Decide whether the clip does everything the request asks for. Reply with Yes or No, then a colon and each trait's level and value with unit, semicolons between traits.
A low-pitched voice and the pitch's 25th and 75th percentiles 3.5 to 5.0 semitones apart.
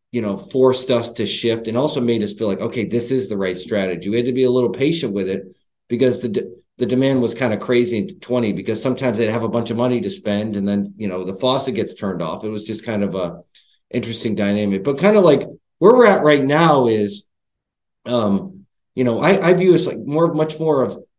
Yes: low, 120 Hz; average, 3.8 semitones